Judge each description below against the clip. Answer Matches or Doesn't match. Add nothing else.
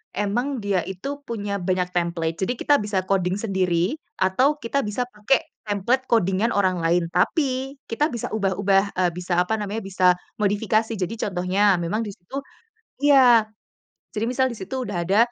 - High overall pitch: Matches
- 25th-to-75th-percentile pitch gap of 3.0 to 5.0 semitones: Matches